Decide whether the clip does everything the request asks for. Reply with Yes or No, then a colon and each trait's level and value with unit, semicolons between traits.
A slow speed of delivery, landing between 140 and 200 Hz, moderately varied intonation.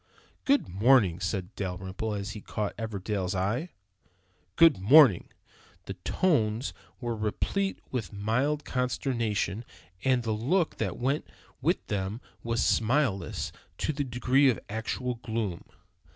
No: slow, 125 wpm; low, 115 Hz; average, 4.8 semitones